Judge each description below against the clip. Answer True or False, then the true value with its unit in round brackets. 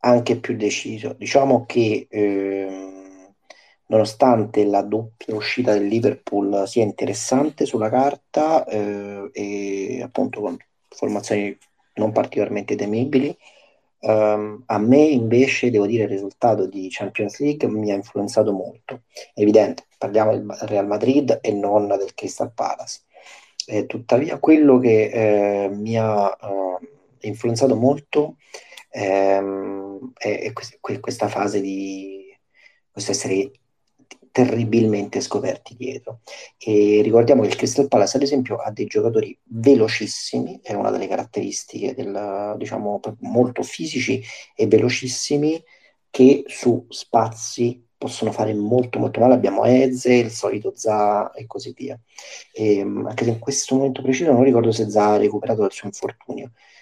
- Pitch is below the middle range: True (110 Hz)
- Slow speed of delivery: False (130 wpm)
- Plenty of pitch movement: False (3.9 semitones)